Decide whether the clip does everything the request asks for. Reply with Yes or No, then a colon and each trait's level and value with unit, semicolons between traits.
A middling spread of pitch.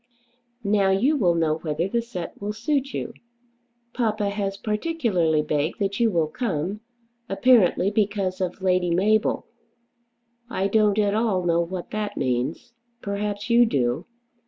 Yes: average, 3.8 semitones